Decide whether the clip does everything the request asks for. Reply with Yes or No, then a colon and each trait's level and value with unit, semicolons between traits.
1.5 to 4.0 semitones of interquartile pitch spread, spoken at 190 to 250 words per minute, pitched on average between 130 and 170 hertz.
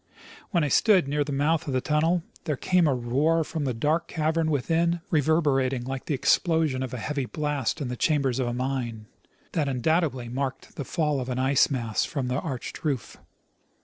Yes: average, 3.6 semitones; average, 195 wpm; medium, 140 Hz